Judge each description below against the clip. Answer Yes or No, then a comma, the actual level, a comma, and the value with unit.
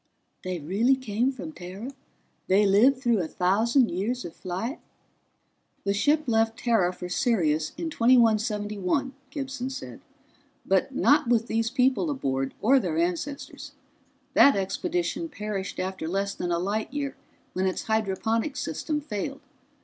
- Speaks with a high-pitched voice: Yes, high, 225 Hz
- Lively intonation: Yes, wide, 5.9 semitones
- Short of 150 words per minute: Yes, average, 140 wpm